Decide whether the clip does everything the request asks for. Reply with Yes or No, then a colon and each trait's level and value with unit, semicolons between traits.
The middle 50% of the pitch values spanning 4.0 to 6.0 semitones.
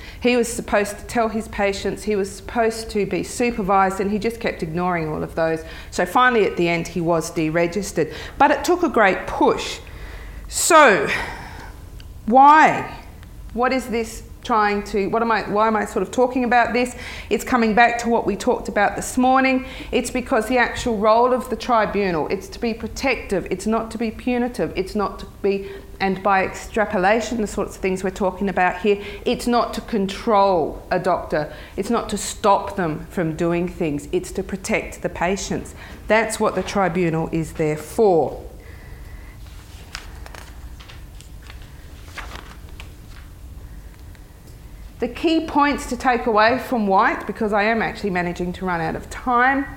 Yes: average, 5.0 semitones